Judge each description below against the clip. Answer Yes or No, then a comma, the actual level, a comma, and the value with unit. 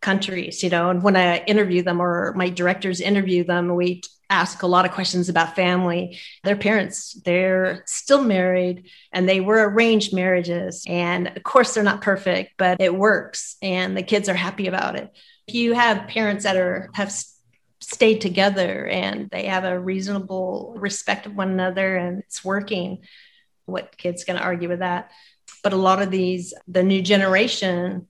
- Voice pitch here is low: No, medium, 185 Hz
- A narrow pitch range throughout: Yes, narrow, 1.8 semitones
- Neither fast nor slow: Yes, average, 175 wpm